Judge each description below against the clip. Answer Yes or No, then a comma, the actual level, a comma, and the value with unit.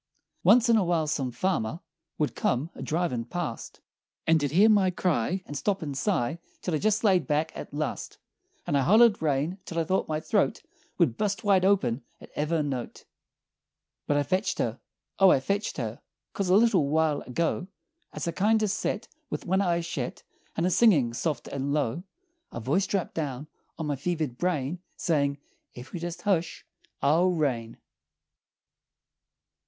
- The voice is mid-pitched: Yes, medium, 165 Hz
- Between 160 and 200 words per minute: Yes, average, 170 wpm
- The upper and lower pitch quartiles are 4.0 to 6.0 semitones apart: Yes, average, 4.8 semitones